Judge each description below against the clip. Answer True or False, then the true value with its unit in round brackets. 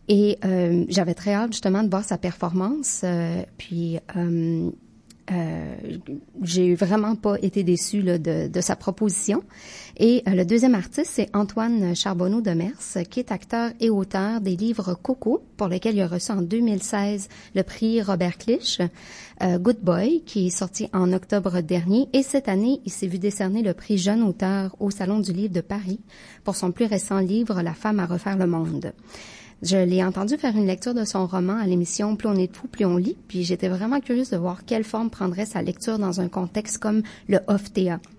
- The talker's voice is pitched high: True (195 Hz)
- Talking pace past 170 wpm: True (195 wpm)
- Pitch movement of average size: True (3.0 semitones)